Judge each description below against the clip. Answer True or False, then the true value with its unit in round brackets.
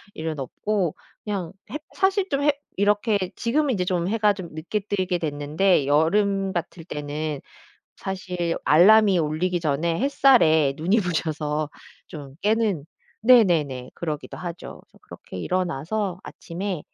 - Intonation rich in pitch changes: False (5.0 semitones)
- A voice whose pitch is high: False (180 Hz)